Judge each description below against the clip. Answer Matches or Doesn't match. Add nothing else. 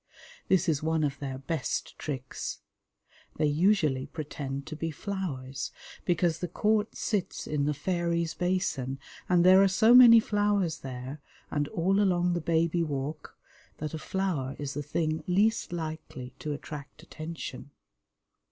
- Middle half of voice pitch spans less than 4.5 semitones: Matches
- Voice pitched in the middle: Matches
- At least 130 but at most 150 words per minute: Matches